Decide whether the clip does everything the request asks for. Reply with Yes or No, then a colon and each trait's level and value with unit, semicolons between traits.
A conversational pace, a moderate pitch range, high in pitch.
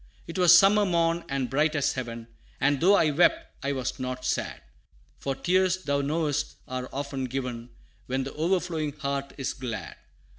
No: average, 160 wpm; average, 4.3 semitones; medium, 140 Hz